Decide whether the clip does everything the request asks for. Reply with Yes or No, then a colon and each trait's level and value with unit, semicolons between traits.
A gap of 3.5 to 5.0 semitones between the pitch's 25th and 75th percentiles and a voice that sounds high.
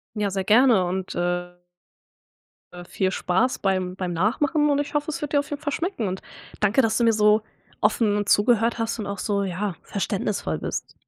Yes: average, 4.4 semitones; high, 210 Hz